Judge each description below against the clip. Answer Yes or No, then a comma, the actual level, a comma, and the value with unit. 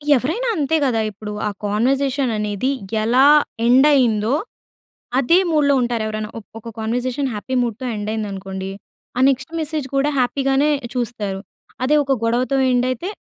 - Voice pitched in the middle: No, very high, 250 Hz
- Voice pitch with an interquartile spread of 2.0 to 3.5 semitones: No, average, 4.1 semitones